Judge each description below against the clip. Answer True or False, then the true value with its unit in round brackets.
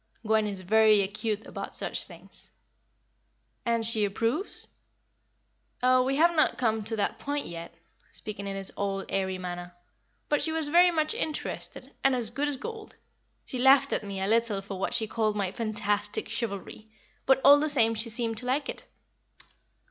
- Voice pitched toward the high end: True (225 Hz)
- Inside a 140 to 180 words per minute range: True (175 wpm)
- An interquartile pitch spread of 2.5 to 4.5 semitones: False (5.0 semitones)